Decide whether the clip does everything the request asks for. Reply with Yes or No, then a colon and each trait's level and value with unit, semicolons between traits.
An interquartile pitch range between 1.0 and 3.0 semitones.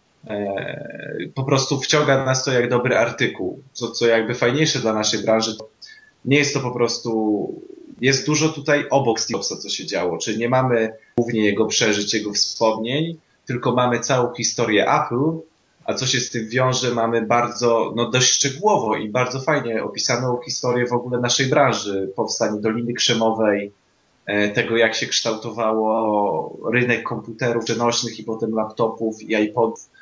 Yes: average, 2.7 semitones